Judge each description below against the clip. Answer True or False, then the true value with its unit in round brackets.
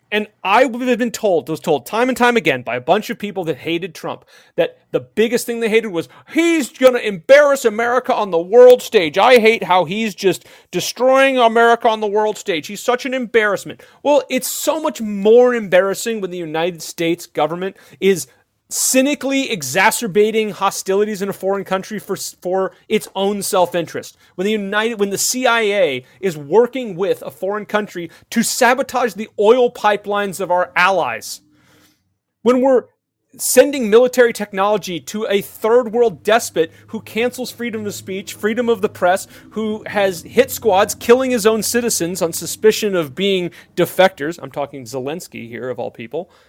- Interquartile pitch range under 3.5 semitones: False (4.6 semitones)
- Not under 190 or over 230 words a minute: False (170 wpm)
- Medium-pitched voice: False (210 Hz)